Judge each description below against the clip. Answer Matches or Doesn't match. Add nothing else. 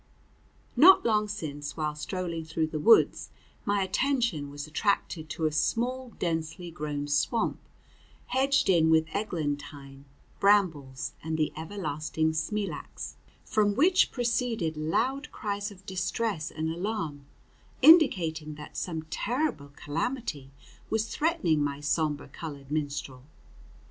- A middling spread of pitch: Doesn't match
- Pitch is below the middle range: Doesn't match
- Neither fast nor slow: Doesn't match